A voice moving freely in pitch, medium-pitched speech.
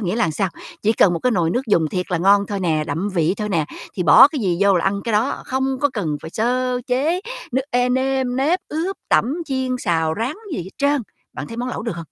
No: wide, 6.4 semitones; high, 220 Hz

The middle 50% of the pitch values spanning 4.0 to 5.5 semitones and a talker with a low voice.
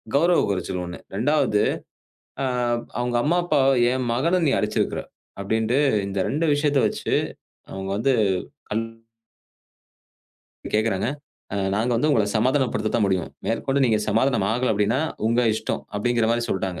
Yes: average, 4.6 semitones; low, 115 Hz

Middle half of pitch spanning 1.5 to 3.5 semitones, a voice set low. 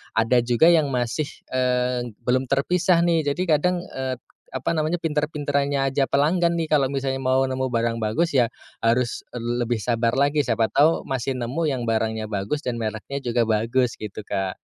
No: average, 4.0 semitones; low, 130 Hz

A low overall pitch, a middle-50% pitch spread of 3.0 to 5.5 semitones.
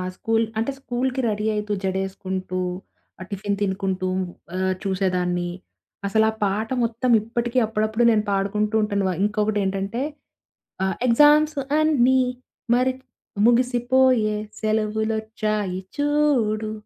No: high, 215 Hz; average, 3.6 semitones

